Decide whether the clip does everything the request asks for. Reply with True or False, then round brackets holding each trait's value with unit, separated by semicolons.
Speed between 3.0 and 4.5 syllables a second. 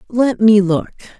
True (4.0 syllables/s)